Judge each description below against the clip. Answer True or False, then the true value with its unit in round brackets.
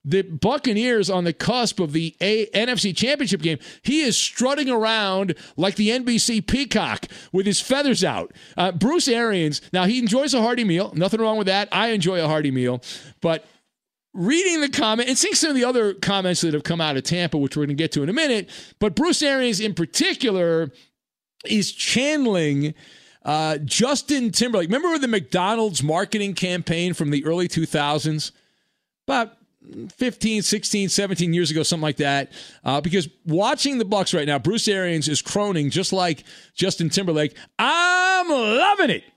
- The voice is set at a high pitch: True (195 Hz)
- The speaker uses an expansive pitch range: True (6.2 semitones)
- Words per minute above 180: False (175 wpm)